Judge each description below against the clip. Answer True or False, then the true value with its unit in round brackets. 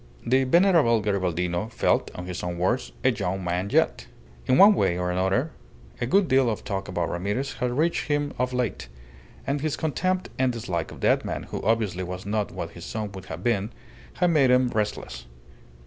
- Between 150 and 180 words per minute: False (195 wpm)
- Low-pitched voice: True (110 Hz)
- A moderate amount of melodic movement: False (6.4 semitones)